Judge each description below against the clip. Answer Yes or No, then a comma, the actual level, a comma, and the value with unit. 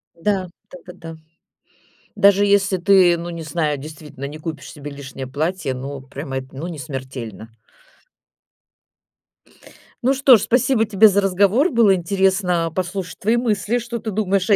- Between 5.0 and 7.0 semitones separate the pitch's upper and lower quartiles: Yes, wide, 5.4 semitones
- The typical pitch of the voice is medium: Yes, medium, 180 Hz